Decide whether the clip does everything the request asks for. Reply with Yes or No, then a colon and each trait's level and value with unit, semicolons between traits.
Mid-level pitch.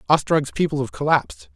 Yes: medium, 145 Hz